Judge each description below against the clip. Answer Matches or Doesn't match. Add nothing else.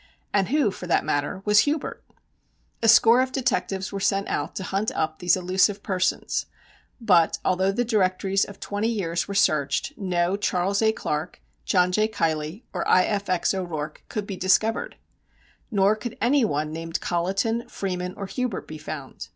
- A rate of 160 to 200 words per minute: Matches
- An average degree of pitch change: Matches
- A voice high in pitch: Matches